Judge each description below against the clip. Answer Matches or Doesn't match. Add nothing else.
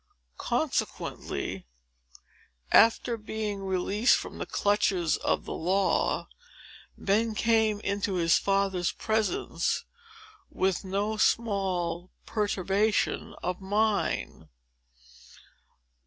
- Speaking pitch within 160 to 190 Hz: Doesn't match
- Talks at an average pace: Doesn't match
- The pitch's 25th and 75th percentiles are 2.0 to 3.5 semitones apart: Matches